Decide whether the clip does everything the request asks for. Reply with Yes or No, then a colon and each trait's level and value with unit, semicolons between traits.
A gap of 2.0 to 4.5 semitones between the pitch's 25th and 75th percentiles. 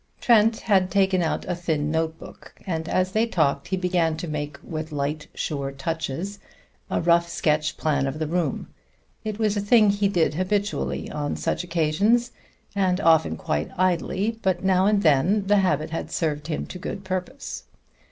Yes: average, 4.2 semitones